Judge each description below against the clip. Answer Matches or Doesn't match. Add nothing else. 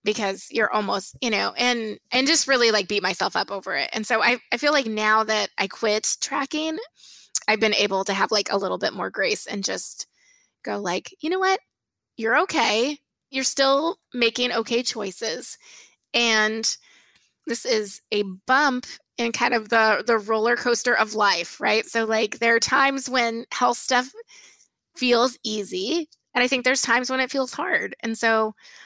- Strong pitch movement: Doesn't match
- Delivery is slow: Doesn't match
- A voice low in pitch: Doesn't match